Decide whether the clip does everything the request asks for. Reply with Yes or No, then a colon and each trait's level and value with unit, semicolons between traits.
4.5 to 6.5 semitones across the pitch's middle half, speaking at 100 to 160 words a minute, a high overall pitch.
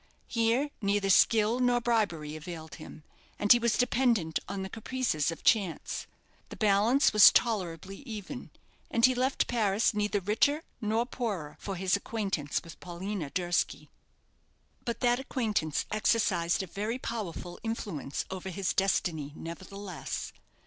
Yes: average, 4.8 semitones; slow, 135 wpm; high, 205 Hz